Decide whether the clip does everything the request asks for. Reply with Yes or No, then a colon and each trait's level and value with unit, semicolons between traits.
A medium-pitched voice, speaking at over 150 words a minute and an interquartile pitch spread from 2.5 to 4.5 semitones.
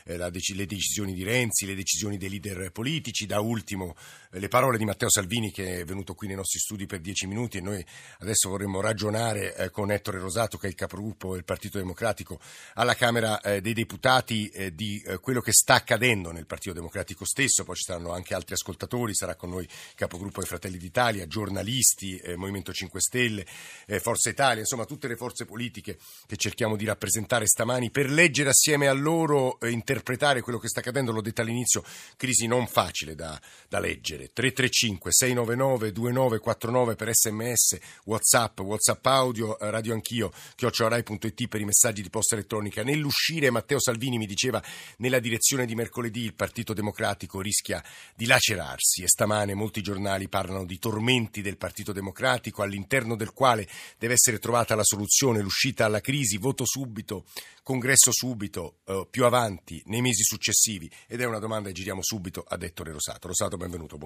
No: low, 110 Hz; fast, 170 wpm; average, 3.8 semitones